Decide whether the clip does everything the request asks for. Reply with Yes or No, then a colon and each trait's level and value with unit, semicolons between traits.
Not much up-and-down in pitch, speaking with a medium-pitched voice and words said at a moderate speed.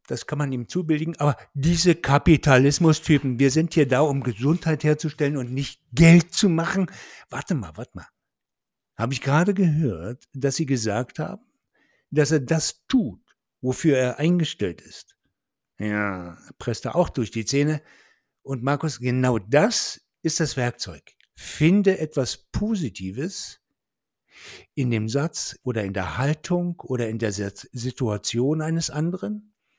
No: average, 4.6 semitones; medium, 145 Hz; average, 145 wpm